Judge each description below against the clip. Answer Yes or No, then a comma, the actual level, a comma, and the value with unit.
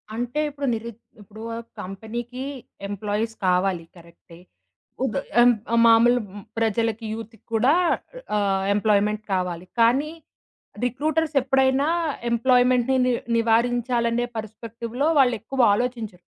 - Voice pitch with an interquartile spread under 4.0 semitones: Yes, average, 2.9 semitones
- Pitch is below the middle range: No, high, 230 Hz